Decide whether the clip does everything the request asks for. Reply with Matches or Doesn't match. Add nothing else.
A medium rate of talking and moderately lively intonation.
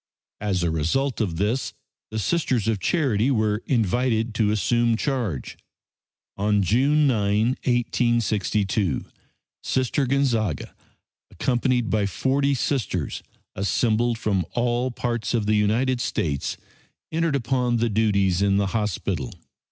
Doesn't match